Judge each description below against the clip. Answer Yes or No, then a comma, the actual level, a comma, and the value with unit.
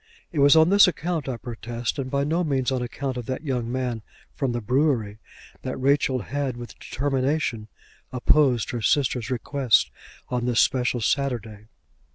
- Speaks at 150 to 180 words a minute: Yes, average, 165 wpm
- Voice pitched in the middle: No, low, 130 Hz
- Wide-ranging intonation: No, average, 2.9 semitones